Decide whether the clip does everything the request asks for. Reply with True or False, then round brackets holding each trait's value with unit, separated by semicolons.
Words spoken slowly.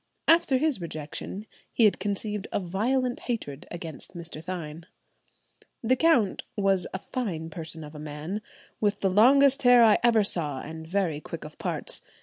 False (160 wpm)